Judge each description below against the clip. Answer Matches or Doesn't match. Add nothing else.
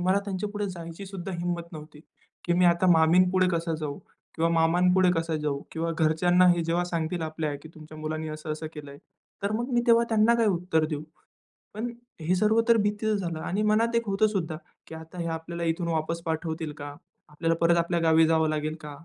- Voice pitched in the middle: Matches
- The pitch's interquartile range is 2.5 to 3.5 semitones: Matches